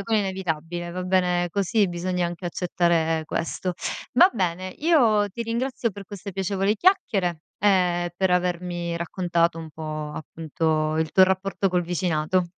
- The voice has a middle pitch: Yes, medium, 180 Hz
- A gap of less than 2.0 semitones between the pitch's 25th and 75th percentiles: No, narrow, 2.5 semitones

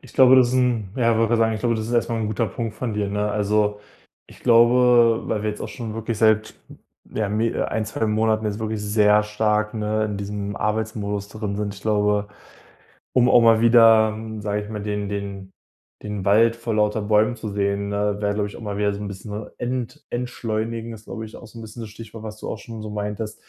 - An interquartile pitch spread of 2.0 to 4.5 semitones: No, narrow, 1.6 semitones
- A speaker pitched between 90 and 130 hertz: Yes, low, 110 Hz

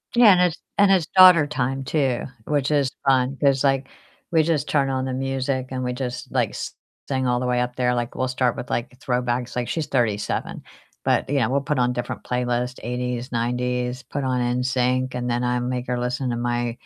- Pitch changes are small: Yes, narrow, 1.8 semitones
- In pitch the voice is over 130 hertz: No, low, 125 Hz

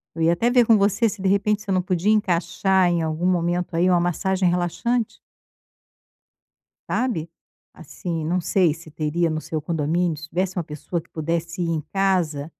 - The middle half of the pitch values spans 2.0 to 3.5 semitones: Yes, average, 2.7 semitones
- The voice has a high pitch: No, medium, 175 Hz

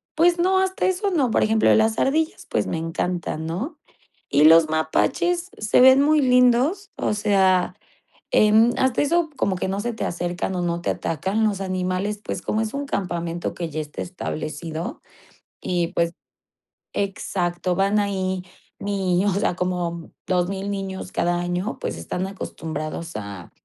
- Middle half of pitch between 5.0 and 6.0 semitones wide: Yes, average, 5.3 semitones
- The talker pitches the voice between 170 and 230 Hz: Yes, high, 190 Hz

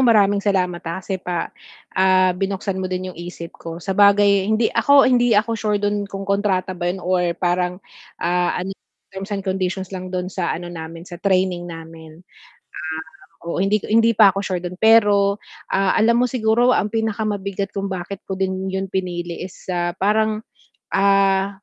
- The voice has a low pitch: No, high, 190 Hz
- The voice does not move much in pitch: Yes, narrow, 2.2 semitones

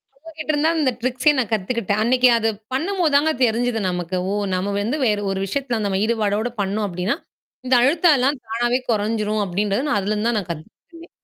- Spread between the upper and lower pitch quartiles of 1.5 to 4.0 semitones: No, average, 4.7 semitones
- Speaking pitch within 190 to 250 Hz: Yes, high, 230 Hz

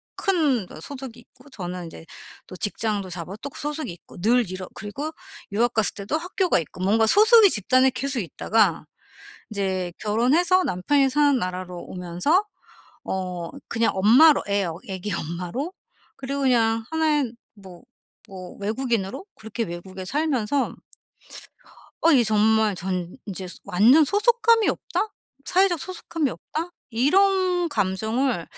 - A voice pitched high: Yes, high, 225 Hz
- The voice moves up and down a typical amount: No, wide, 7.7 semitones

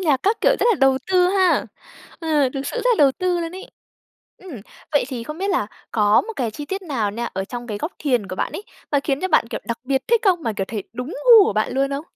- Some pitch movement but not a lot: No, wide, 7.7 semitones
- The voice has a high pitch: Yes, very high, 285 Hz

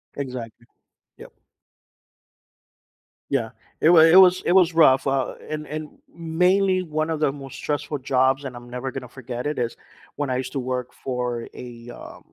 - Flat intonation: No, average, 4.0 semitones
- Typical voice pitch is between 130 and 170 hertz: Yes, low, 135 Hz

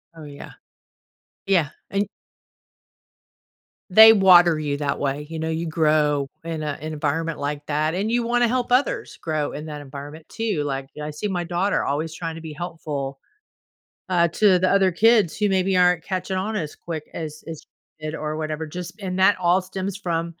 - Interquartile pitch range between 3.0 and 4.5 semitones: Yes, average, 3.8 semitones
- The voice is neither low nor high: Yes, medium, 165 Hz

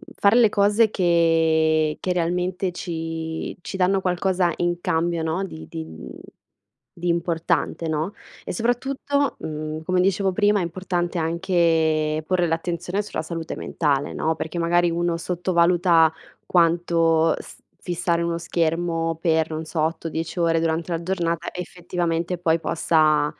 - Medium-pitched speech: Yes, medium, 170 Hz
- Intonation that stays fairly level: Yes, narrow, 1.8 semitones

